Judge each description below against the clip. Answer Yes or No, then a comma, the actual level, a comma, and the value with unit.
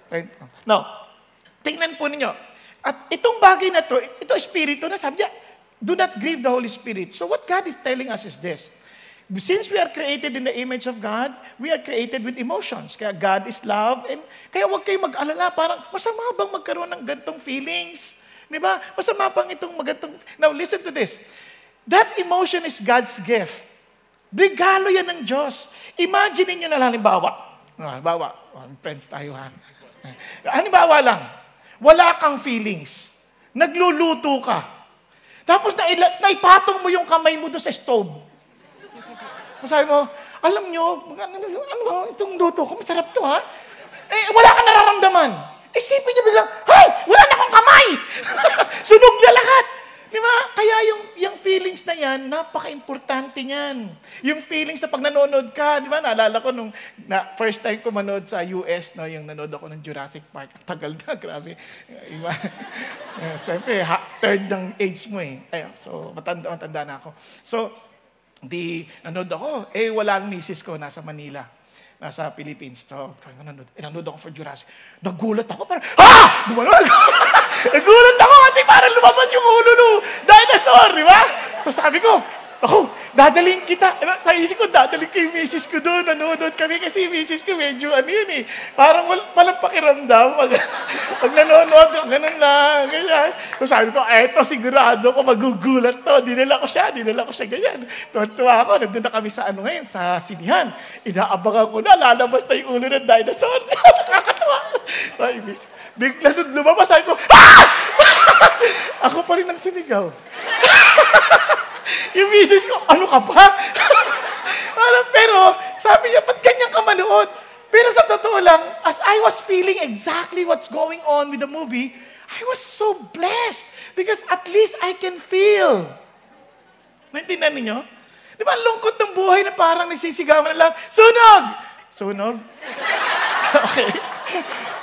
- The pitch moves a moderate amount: No, wide, 8.3 semitones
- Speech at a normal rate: Yes, average, 160 wpm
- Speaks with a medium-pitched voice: No, very high, 305 Hz